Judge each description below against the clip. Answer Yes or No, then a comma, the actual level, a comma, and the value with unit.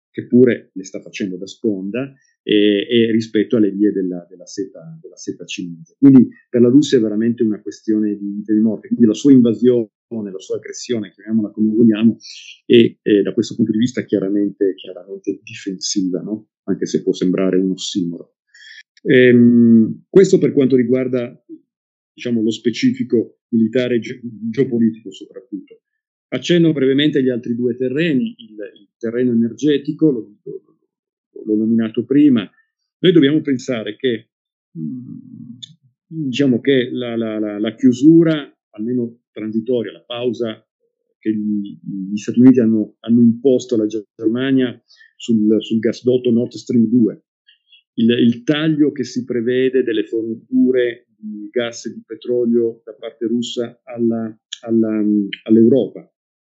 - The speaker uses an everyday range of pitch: Yes, average, 3.6 semitones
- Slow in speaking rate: No, average, 140 wpm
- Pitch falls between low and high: No, low, 120 Hz